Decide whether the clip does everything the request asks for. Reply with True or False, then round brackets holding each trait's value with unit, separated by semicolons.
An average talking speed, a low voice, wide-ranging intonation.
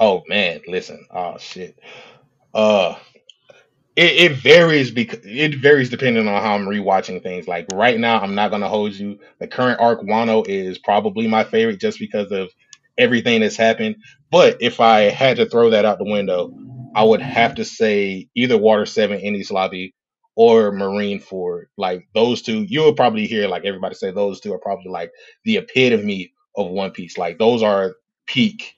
True (180 wpm; 115 Hz; 6.8 semitones)